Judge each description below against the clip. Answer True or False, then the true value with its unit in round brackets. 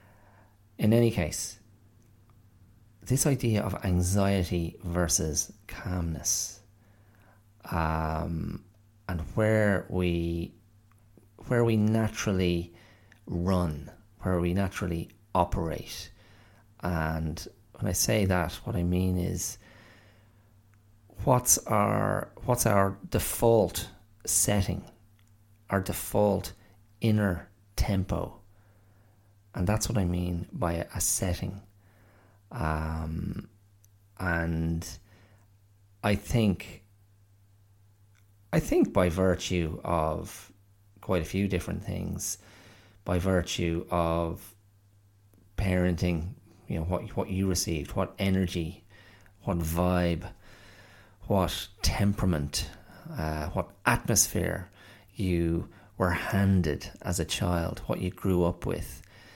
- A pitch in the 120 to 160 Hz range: False (100 Hz)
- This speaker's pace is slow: True (95 wpm)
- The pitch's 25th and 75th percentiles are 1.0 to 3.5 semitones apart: True (2.7 semitones)